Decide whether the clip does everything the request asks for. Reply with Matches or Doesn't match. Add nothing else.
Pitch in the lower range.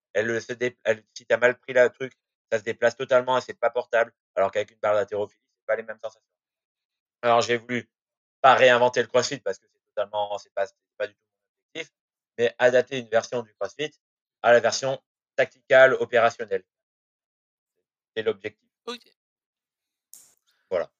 Matches